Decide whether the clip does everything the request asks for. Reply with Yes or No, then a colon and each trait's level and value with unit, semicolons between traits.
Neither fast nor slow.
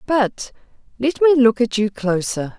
Yes: average, 165 wpm